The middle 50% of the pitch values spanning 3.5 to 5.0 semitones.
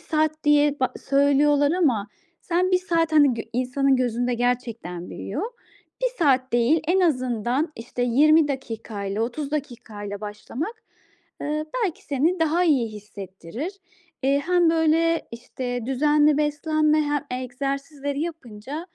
Yes: average, 4.2 semitones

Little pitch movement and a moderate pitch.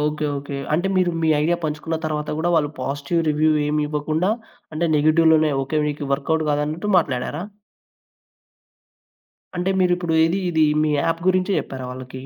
Yes: narrow, 2.2 semitones; medium, 155 Hz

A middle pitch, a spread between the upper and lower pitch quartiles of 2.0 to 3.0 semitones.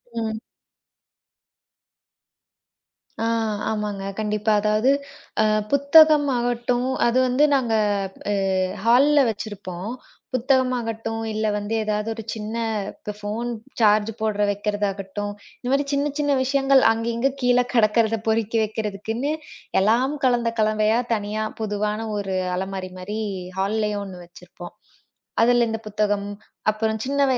No: high, 220 Hz; average, 2.7 semitones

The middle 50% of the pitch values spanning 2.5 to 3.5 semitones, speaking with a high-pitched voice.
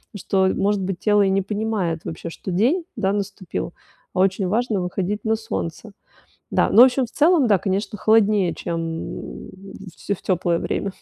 Yes: average, 2.9 semitones; high, 195 Hz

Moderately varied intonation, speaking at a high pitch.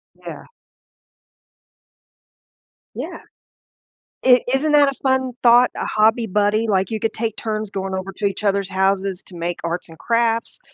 Yes: average, 3.4 semitones; high, 215 Hz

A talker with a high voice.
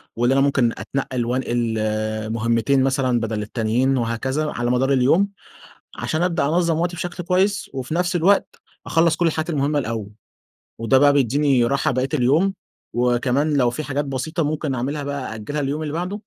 No: medium, 140 Hz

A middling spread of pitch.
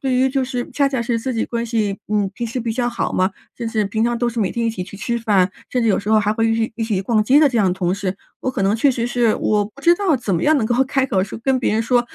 Yes: average, 3.2 semitones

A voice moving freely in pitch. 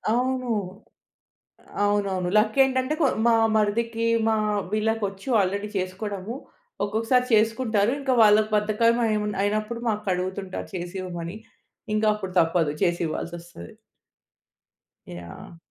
No: average, 3.4 semitones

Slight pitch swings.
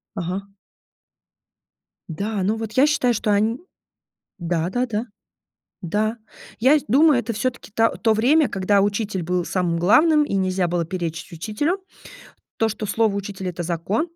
No: average, 4.3 semitones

